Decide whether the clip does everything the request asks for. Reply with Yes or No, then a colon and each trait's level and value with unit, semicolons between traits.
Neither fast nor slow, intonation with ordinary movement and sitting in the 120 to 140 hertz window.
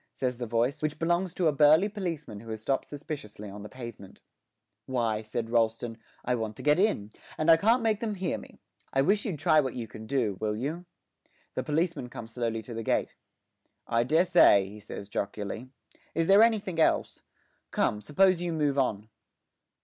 No: average, 190 wpm; wide, 7.0 semitones; low, 135 Hz